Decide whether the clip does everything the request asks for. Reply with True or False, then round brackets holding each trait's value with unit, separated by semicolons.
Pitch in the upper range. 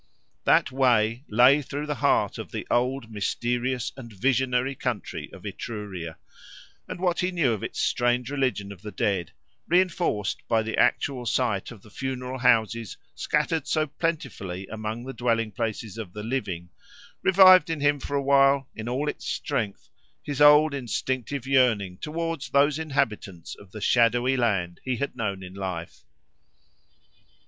False (125 Hz)